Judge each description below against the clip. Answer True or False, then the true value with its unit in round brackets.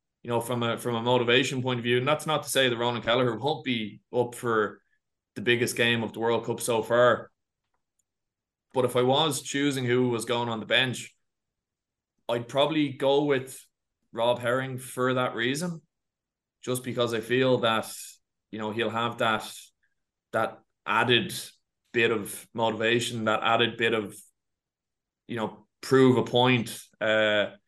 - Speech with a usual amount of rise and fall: False (2.0 semitones)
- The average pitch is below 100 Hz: False (120 Hz)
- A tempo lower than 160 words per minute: False (165 wpm)